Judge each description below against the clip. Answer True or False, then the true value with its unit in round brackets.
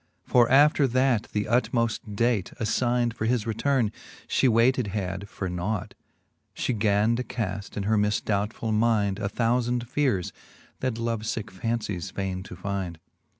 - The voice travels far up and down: False (3.0 semitones)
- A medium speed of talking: True (150 wpm)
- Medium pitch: False (110 Hz)